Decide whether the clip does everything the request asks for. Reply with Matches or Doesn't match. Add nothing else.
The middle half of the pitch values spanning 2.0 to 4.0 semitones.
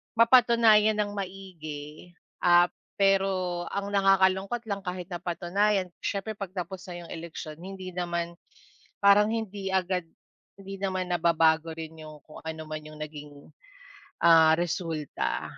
Matches